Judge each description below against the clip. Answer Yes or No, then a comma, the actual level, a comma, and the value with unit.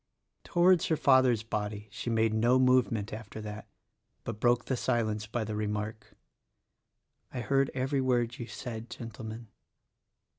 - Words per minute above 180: No, average, 145 wpm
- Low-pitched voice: Yes, low, 115 Hz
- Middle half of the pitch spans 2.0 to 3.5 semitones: Yes, average, 2.9 semitones